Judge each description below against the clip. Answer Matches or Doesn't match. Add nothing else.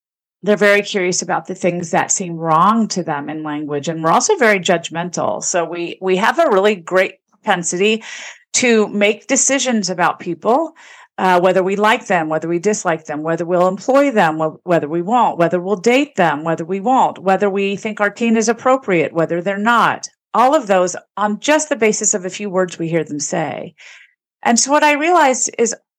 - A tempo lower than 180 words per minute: Doesn't match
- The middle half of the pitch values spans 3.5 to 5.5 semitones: Matches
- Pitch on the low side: Doesn't match